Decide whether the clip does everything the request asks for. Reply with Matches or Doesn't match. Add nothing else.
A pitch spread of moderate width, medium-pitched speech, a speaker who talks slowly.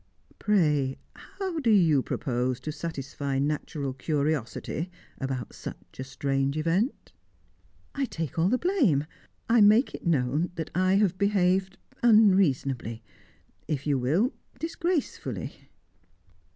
Doesn't match